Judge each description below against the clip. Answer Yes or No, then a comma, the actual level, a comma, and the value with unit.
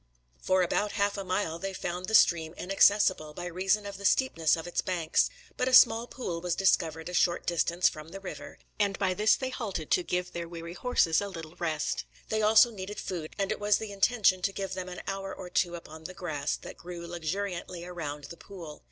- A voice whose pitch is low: No, medium, 180 Hz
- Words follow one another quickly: Yes, fast, 215 wpm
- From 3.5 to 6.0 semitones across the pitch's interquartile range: No, average, 3.0 semitones